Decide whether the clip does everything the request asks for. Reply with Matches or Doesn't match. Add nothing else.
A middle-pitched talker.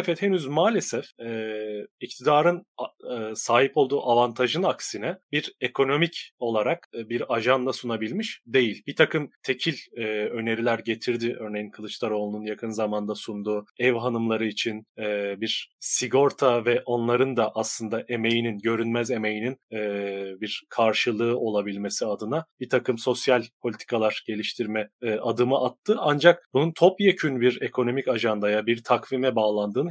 Doesn't match